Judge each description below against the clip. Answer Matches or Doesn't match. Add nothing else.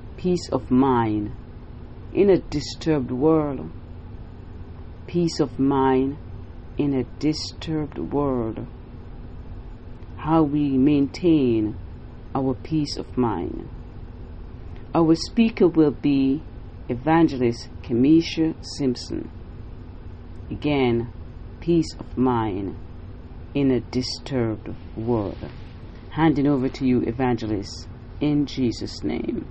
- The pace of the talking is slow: Matches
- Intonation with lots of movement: Matches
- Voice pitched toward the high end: Doesn't match